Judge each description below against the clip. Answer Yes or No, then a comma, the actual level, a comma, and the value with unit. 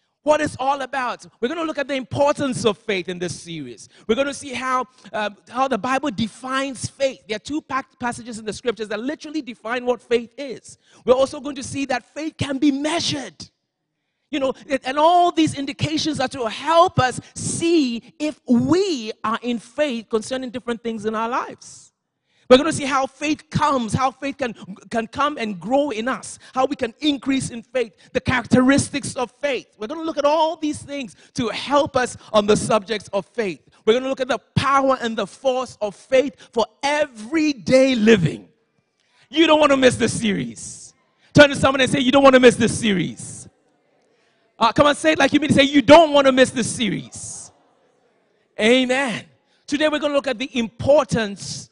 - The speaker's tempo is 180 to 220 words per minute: Yes, average, 195 wpm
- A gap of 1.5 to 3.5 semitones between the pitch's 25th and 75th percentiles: No, average, 3.9 semitones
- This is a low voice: No, very high, 255 Hz